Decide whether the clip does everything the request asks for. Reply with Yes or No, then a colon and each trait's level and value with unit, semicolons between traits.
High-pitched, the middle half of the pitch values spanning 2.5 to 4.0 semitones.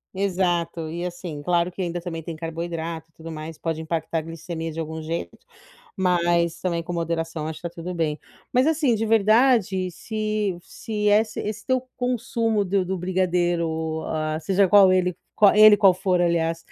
No: medium, 175 Hz; average, 3.4 semitones